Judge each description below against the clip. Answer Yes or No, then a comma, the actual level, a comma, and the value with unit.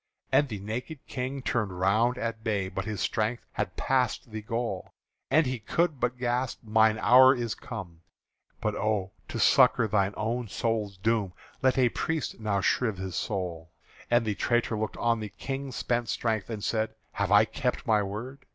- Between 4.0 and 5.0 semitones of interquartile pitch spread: No, average, 3.0 semitones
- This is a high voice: No, low, 110 Hz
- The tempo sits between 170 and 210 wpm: Yes, average, 180 wpm